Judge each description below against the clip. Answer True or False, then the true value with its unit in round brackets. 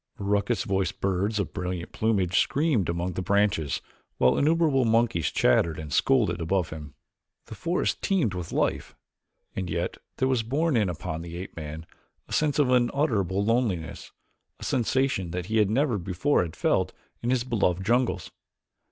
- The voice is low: True (100 Hz)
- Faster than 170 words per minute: False (160 wpm)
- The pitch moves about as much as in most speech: False (6.0 semitones)